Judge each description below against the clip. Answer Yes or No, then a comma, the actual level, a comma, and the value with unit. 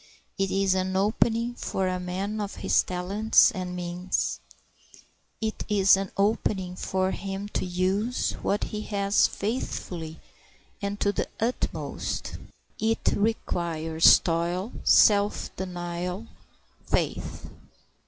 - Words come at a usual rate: No, slow, 115 wpm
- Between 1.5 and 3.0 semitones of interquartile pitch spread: Yes, narrow, 2.5 semitones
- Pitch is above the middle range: Yes, high, 195 Hz